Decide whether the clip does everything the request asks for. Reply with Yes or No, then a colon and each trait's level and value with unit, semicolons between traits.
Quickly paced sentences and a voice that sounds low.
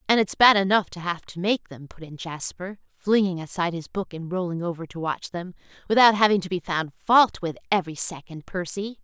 No: fast, 215 wpm; medium, 180 Hz